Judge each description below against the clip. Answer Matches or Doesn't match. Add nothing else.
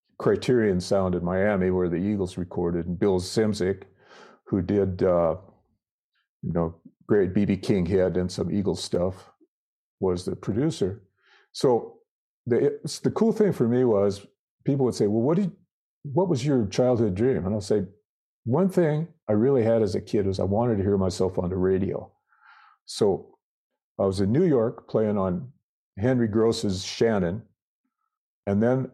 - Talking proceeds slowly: Doesn't match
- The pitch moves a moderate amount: Doesn't match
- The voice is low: Matches